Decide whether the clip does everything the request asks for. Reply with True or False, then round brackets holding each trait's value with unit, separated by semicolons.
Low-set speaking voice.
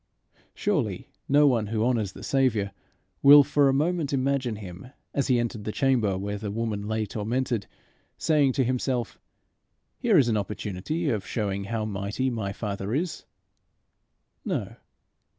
True (115 Hz)